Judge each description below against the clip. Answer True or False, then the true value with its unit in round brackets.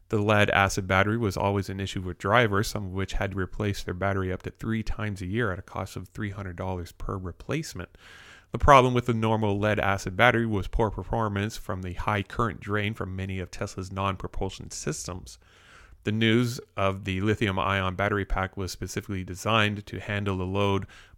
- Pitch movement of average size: False (2.3 semitones)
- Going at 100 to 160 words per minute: False (195 wpm)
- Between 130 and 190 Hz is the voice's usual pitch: False (100 Hz)